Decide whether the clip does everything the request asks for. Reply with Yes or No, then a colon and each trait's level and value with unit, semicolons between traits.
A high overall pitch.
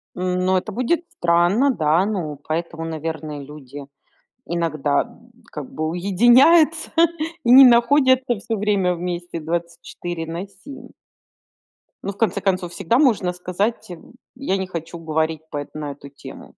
No: medium, 180 Hz